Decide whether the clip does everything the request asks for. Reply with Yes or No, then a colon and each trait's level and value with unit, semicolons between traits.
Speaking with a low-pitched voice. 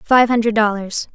No: high, 220 Hz